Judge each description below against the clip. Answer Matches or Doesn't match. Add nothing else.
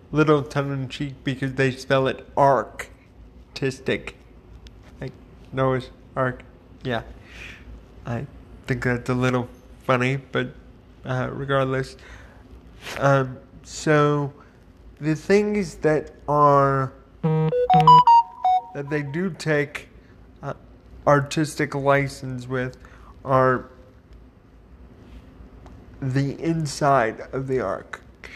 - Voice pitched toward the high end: Doesn't match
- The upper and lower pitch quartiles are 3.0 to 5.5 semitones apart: Doesn't match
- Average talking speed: Doesn't match